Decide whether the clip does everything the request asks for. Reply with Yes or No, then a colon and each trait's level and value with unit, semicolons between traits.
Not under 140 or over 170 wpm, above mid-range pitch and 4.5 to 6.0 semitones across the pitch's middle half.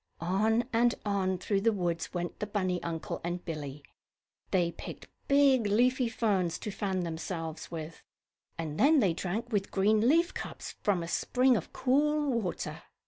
Yes: average, 160 wpm; high, 200 Hz; wide, 5.5 semitones